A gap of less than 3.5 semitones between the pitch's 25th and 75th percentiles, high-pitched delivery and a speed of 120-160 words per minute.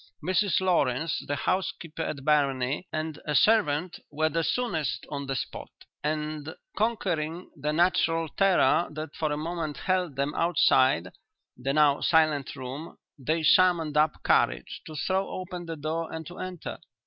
No: average, 3.1 semitones; medium, 155 Hz; average, 150 wpm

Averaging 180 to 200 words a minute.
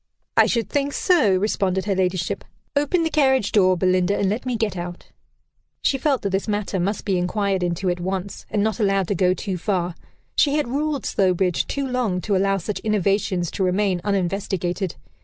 Yes: average, 190 wpm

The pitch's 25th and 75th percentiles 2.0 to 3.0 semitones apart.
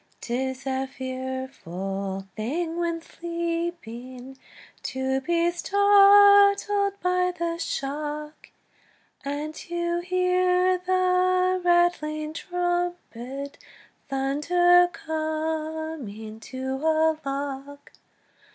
No: average, 4.8 semitones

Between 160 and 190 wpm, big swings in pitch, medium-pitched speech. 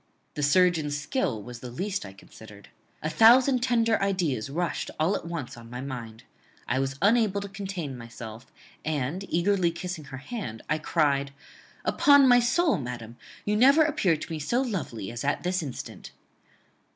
Yes: average, 165 wpm; wide, 8.0 semitones; medium, 160 Hz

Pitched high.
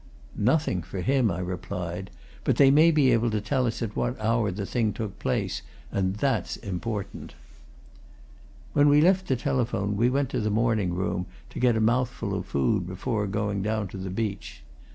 No: low, 110 Hz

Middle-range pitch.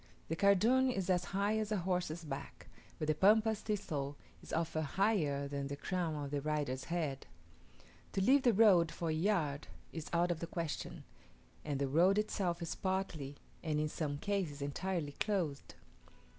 Yes: medium, 170 Hz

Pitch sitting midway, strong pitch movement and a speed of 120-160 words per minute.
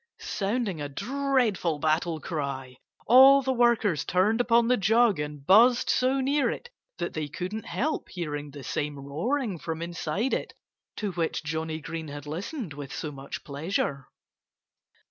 Yes: medium, 175 Hz; wide, 8.1 semitones; average, 150 wpm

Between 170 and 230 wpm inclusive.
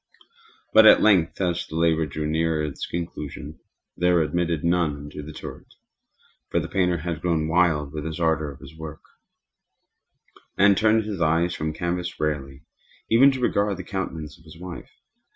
Yes: average, 175 wpm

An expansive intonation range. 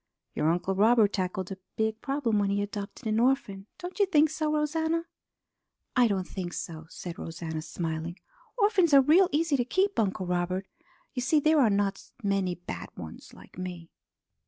Yes: wide, 8.4 semitones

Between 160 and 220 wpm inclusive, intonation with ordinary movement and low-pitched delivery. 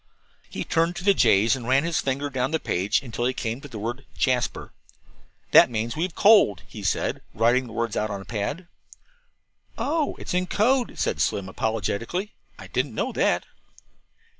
No: average, 185 wpm; wide, 6.7 semitones; low, 125 Hz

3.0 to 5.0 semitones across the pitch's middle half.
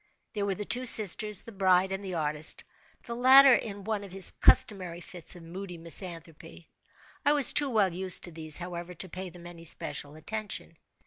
Yes: average, 3.6 semitones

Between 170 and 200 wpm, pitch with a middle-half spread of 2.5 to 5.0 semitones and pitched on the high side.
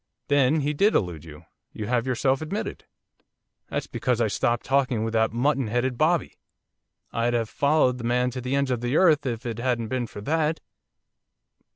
No: average, 185 wpm; average, 3.4 semitones; low, 125 Hz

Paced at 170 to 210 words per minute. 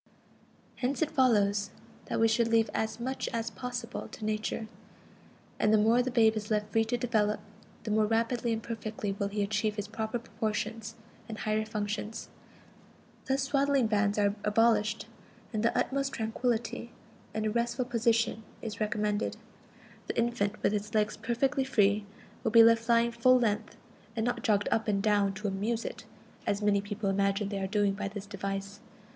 Yes: average, 175 wpm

